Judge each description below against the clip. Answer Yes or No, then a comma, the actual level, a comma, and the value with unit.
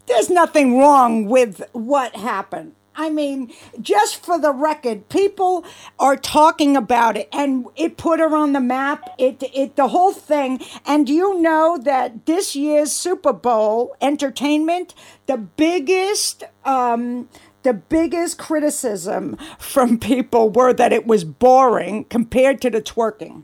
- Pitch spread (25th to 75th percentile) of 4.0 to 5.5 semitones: Yes, average, 4.6 semitones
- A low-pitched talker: No, very high, 280 Hz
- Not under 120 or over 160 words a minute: Yes, average, 140 wpm